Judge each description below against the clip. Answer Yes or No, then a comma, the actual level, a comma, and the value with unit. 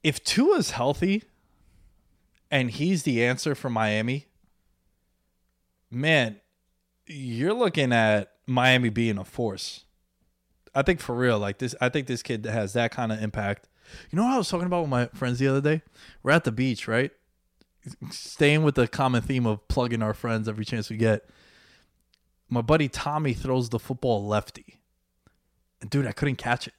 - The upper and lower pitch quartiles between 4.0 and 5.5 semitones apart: Yes, average, 4.5 semitones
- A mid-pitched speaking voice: No, low, 120 Hz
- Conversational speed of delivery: Yes, average, 170 wpm